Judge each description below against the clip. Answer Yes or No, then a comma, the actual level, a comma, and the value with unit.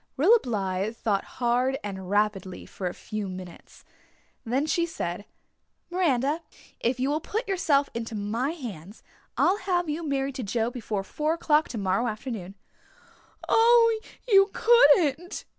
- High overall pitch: Yes, very high, 255 Hz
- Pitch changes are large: Yes, wide, 8.0 semitones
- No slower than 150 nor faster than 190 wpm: No, average, 140 wpm